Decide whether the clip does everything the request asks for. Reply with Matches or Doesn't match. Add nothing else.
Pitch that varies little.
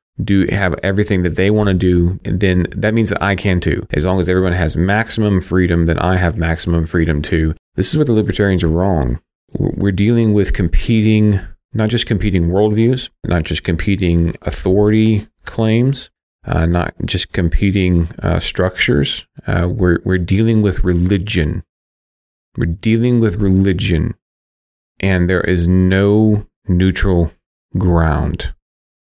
Doesn't match